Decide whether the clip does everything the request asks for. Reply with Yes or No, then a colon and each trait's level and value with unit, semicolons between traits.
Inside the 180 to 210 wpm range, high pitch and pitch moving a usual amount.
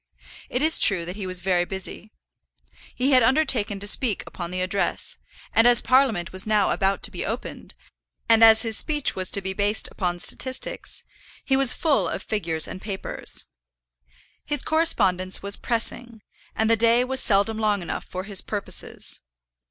No: average, 170 wpm; high, 215 Hz; average, 4.2 semitones